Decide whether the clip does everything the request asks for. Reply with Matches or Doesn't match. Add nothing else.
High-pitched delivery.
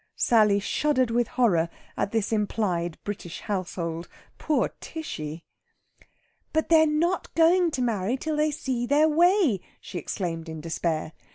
Matches